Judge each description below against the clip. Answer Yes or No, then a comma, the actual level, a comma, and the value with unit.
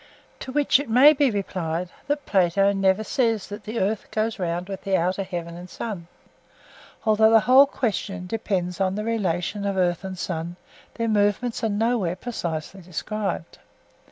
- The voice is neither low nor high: No, high, 200 Hz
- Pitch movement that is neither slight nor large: Yes, average, 3.8 semitones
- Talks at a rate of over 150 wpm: Yes, average, 165 wpm